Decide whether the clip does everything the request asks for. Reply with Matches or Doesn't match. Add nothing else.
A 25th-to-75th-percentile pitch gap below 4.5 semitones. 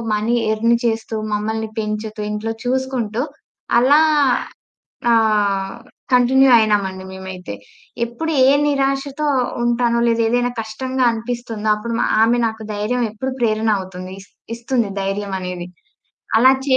Matches